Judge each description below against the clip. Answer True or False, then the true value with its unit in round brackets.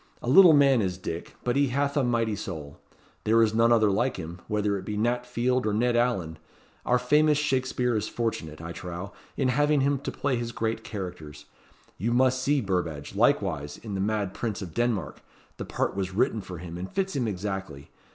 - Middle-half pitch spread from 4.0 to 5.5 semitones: True (5.1 semitones)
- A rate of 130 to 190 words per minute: False (200 wpm)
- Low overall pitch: True (110 Hz)